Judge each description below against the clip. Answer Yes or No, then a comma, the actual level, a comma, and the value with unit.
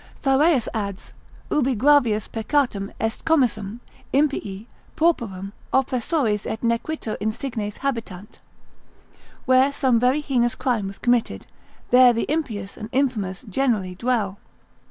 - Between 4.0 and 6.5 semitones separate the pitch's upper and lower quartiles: Yes, average, 4.4 semitones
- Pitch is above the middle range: Yes, high, 235 Hz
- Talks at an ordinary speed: No, slow, 115 wpm